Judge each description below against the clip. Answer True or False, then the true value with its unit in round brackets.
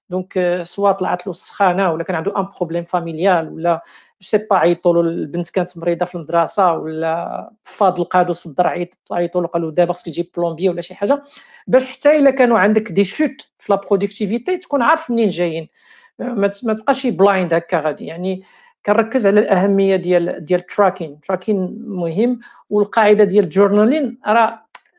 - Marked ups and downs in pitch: False (3.9 semitones)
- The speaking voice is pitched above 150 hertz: True (190 Hz)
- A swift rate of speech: True (160 wpm)